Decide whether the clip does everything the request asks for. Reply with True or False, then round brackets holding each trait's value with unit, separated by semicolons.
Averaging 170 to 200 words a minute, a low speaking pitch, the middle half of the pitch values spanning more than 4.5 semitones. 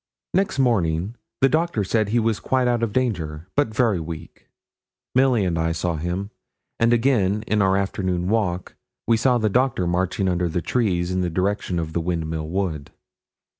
True (175 wpm; 95 Hz; 5.0 semitones)